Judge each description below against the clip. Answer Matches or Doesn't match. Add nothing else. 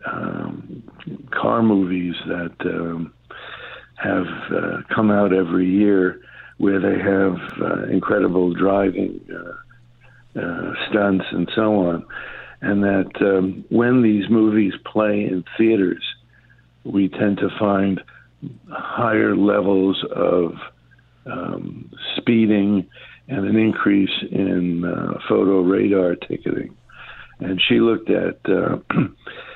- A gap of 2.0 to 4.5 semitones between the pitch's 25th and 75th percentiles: Matches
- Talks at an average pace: Doesn't match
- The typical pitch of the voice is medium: Doesn't match